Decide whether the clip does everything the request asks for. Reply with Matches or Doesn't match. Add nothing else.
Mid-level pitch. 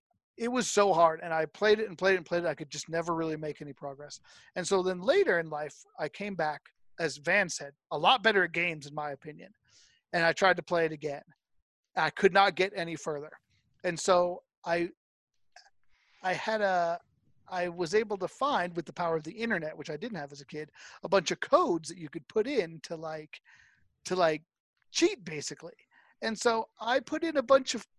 Matches